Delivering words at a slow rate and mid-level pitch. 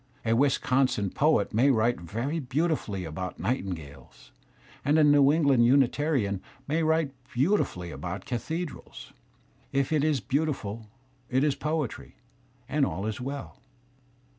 No: slow, 130 wpm; low, 130 Hz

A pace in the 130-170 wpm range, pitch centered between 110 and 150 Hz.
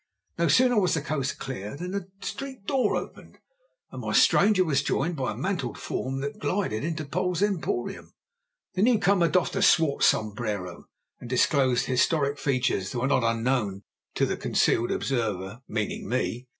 Yes: average, 165 wpm; medium, 140 Hz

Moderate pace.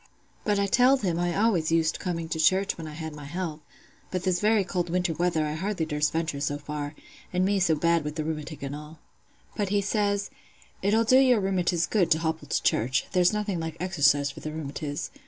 No: fast, 210 wpm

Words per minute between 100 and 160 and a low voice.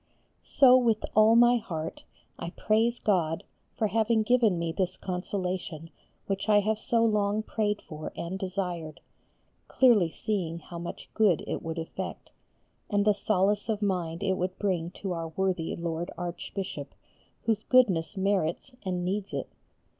No: average, 150 wpm; high, 190 Hz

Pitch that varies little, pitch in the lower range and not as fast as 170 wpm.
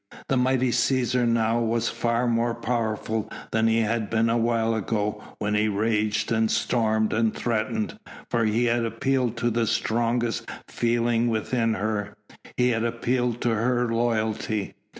Yes: narrow, 1.4 semitones; low, 115 Hz; average, 150 wpm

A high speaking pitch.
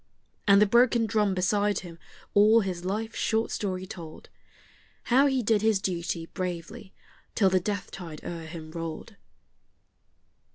Yes: high, 195 Hz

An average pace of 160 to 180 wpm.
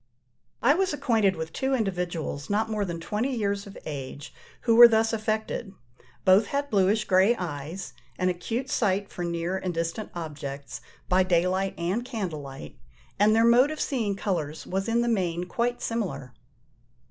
Yes: average, 170 wpm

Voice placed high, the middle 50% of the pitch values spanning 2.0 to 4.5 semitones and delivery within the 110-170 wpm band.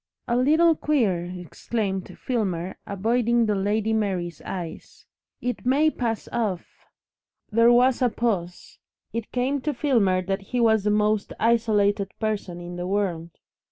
Yes: high, 215 Hz; average, 4.0 semitones; average, 145 wpm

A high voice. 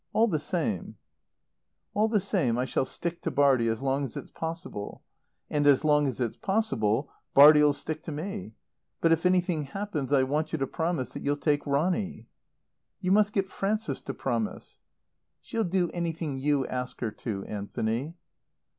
No: medium, 150 Hz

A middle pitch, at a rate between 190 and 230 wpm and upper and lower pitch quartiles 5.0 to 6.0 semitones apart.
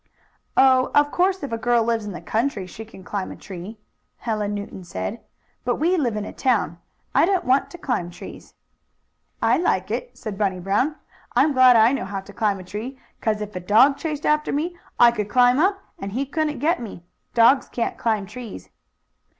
No: high, 230 Hz; average, 200 wpm; wide, 5.4 semitones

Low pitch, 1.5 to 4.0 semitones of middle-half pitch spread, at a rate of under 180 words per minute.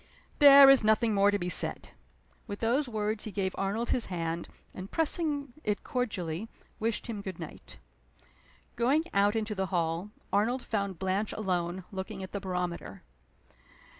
No: high, 205 Hz; average, 3.7 semitones; average, 155 wpm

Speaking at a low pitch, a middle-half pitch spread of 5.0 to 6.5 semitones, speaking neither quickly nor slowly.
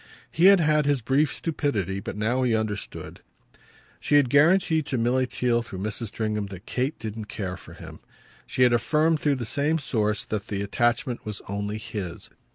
Yes: low, 120 Hz; average, 5.3 semitones; average, 180 wpm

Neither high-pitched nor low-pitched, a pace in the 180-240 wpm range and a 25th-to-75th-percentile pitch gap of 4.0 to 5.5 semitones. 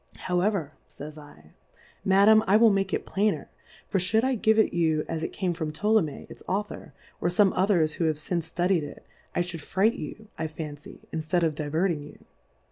Yes: medium, 175 Hz; average, 190 wpm; average, 4.4 semitones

